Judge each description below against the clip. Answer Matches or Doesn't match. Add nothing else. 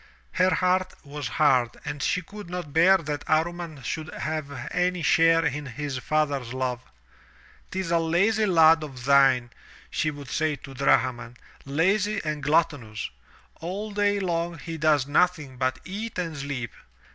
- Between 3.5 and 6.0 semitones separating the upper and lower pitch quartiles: Matches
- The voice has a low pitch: Doesn't match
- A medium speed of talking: Matches